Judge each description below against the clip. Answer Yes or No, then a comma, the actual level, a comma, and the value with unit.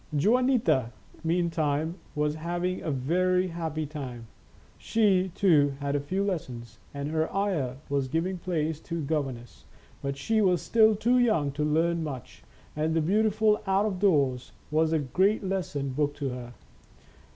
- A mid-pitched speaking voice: Yes, medium, 160 Hz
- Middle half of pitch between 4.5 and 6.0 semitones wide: Yes, average, 4.8 semitones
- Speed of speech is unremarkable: Yes, average, 160 wpm